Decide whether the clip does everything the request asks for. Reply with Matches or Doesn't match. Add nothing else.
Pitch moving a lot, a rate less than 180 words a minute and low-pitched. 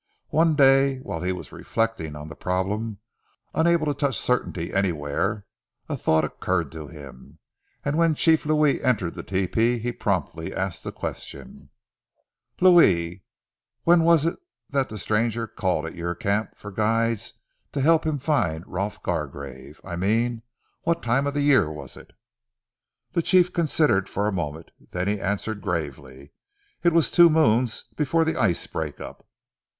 Matches